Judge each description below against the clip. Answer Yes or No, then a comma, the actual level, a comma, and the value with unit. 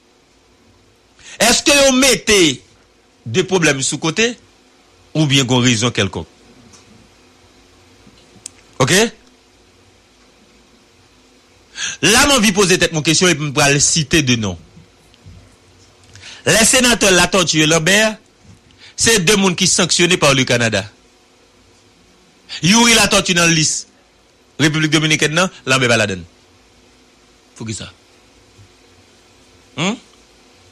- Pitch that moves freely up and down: Yes, wide, 8.5 semitones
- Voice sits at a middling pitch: No, low, 125 Hz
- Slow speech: Yes, slow, 105 wpm